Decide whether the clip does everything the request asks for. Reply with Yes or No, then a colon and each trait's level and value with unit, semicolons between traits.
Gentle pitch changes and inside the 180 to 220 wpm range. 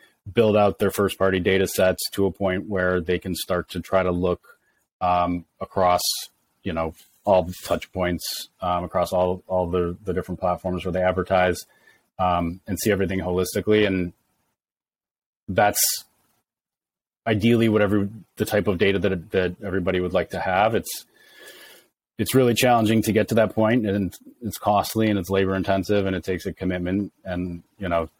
No: narrow, 2.1 semitones; average, 170 wpm